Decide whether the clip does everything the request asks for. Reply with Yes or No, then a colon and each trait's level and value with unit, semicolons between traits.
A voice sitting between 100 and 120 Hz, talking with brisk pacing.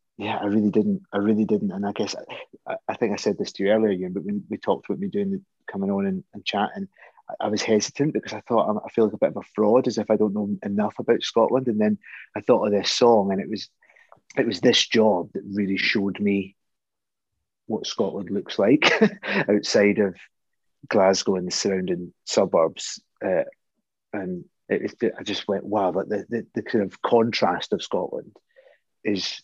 Yes: low, 105 Hz; fast, 210 wpm